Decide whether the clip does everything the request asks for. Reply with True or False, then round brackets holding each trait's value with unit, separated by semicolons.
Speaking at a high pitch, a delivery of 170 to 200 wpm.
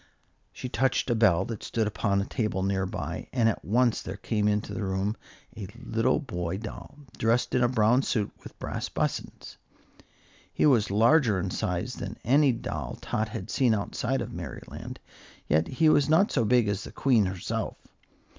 False (110 Hz; 180 wpm)